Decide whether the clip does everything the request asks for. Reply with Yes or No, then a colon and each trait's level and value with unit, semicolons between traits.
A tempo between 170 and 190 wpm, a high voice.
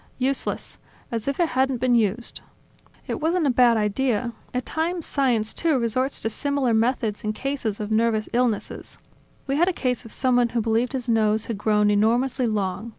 Yes: average, 180 wpm; high, 240 Hz